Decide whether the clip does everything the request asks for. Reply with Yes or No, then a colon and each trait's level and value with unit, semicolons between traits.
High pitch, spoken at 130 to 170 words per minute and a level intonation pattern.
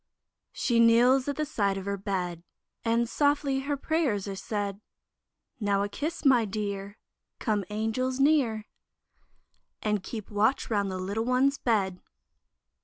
No: high, 220 Hz; average, 140 wpm; average, 4.6 semitones